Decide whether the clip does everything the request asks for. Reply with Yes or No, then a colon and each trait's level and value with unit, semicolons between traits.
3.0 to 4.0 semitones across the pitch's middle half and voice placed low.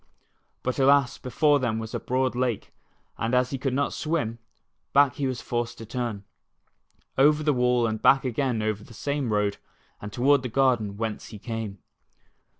Yes: average, 3.4 semitones; low, 125 Hz